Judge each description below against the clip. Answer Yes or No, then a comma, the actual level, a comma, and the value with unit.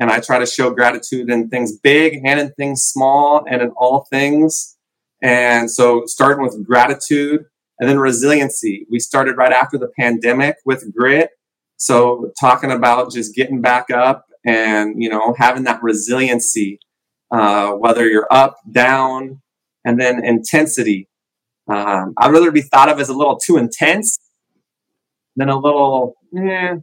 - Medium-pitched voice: No, low, 125 Hz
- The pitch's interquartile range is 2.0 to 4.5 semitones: Yes, average, 2.7 semitones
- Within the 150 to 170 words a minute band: Yes, average, 155 wpm